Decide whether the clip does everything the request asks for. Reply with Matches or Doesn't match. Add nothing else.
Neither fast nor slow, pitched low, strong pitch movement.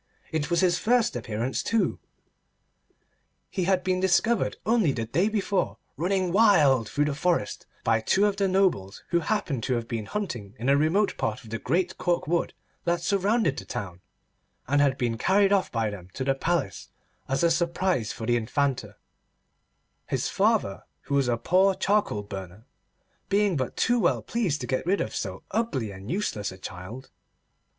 Doesn't match